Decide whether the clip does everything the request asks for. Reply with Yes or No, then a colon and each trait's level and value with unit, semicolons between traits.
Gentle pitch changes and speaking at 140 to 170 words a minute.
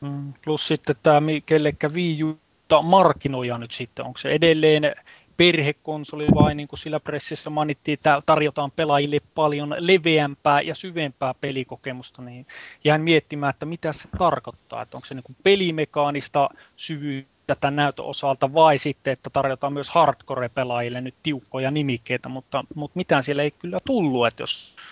Yes: narrow, 2.1 semitones; average, 145 wpm